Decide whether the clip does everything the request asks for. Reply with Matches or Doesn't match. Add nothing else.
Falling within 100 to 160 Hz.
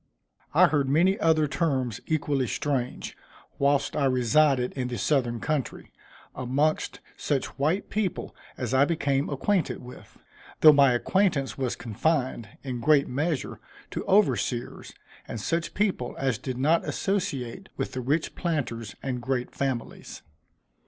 Matches